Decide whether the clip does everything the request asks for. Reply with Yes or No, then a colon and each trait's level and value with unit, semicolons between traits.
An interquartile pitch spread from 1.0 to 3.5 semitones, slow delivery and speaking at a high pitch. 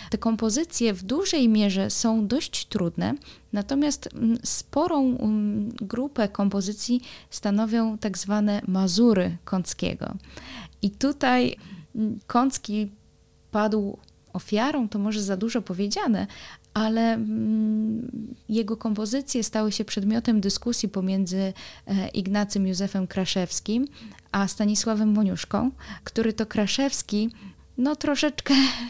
Yes: average, 2.8 semitones; slow, 95 wpm; high, 220 Hz